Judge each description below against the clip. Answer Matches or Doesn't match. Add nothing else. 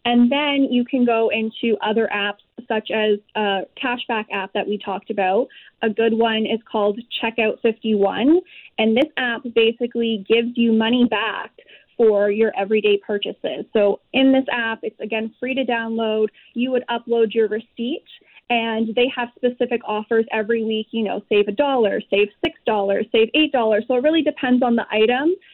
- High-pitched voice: Matches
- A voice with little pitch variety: Matches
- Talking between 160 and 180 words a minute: Matches